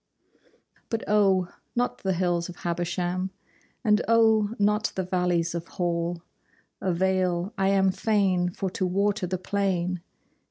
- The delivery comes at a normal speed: No, slow, 130 wpm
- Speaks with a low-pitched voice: No, medium, 185 Hz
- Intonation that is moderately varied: No, narrow, 2.3 semitones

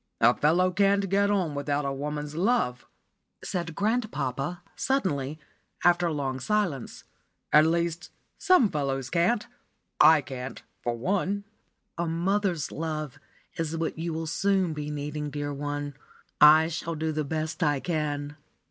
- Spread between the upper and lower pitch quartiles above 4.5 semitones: No, average, 3.5 semitones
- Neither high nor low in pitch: Yes, medium, 160 Hz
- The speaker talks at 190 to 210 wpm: No, average, 140 wpm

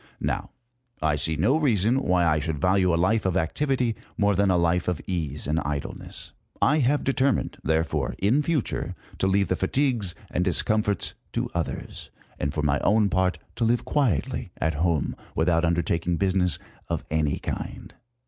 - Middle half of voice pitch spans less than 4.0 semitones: No, average, 5.2 semitones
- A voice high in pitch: No, very low, 90 Hz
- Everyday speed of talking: Yes, average, 165 wpm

